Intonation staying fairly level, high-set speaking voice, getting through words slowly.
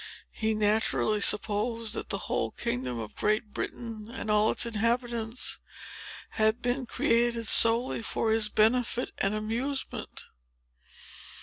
Yes: narrow, 1.8 semitones; high, 225 Hz; slow, 120 wpm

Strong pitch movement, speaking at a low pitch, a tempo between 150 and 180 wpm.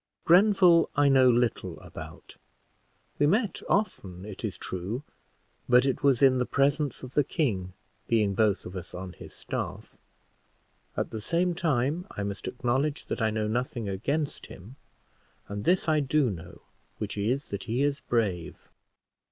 Yes: wide, 6.1 semitones; low, 125 Hz; average, 160 wpm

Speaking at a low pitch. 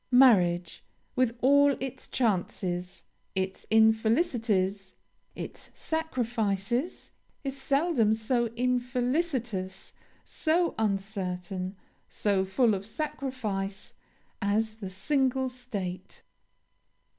No: high, 220 Hz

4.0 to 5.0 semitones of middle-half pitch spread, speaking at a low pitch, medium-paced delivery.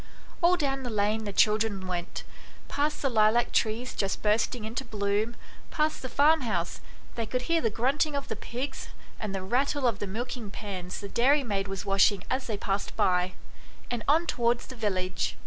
No: average, 4.5 semitones; high, 225 Hz; average, 185 wpm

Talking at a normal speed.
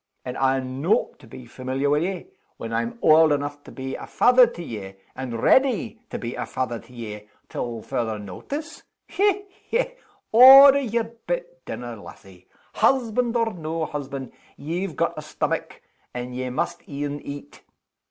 Yes: average, 160 wpm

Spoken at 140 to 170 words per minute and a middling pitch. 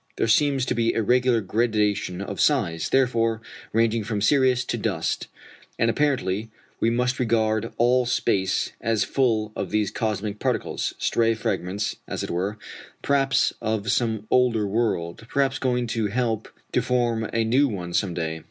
No: average, 160 wpm; low, 115 Hz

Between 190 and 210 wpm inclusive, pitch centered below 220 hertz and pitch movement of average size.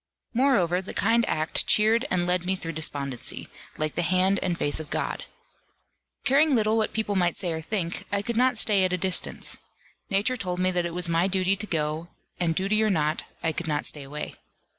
Yes: fast, 205 wpm; medium, 185 Hz; average, 4.3 semitones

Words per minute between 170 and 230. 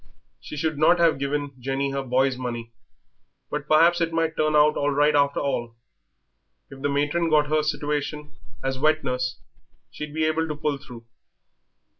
Yes: average, 175 wpm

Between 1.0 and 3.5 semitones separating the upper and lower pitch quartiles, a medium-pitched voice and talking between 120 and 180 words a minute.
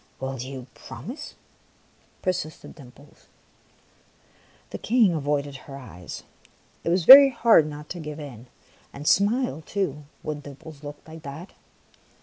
No: average, 4.7 semitones; medium, 150 Hz; slow, 135 wpm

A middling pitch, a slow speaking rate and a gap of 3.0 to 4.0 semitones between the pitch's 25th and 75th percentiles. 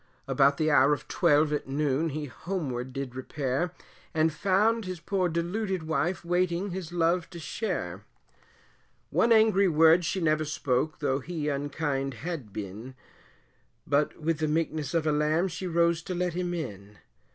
No: medium, 160 Hz; average, 160 wpm; average, 3.6 semitones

